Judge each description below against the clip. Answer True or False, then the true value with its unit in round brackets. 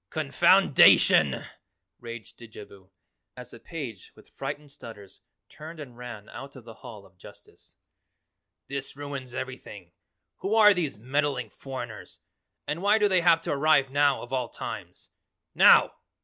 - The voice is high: False (135 Hz)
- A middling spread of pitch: True (4.4 semitones)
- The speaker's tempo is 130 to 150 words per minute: True (140 wpm)